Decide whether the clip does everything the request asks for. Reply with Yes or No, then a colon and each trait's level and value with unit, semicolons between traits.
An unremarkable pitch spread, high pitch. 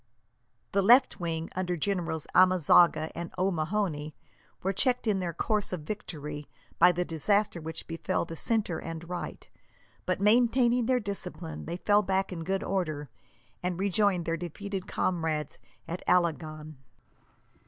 No: average, 3.6 semitones; medium, 180 Hz